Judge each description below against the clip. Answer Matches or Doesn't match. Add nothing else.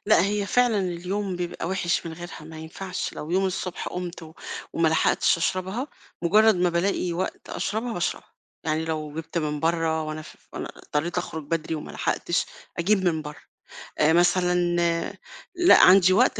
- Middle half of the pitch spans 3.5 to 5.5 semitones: Doesn't match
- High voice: Doesn't match